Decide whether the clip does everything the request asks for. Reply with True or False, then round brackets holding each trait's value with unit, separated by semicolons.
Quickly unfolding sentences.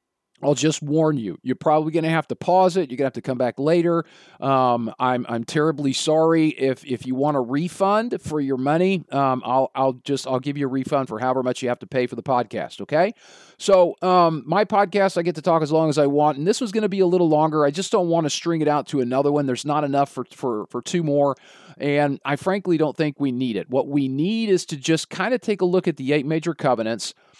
True (260 wpm)